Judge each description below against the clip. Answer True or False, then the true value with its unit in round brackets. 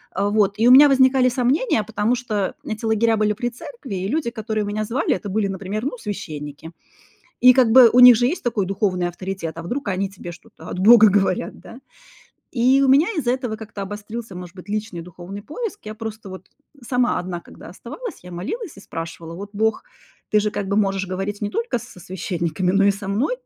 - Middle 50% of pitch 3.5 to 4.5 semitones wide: True (4.1 semitones)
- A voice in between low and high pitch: False (210 Hz)